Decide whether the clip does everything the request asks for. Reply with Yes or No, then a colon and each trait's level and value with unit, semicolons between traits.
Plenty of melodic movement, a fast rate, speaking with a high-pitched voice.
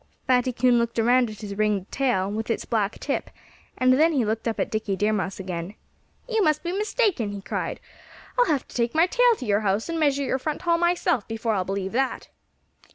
Yes: wide, 6.6 semitones; fast, 220 wpm; high, 240 Hz